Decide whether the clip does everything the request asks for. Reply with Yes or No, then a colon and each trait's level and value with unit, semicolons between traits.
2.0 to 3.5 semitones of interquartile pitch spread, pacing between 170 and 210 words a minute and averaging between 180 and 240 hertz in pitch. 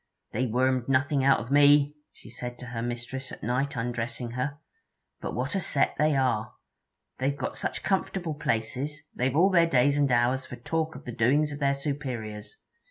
No: average, 3.0 semitones; average, 185 wpm; low, 130 Hz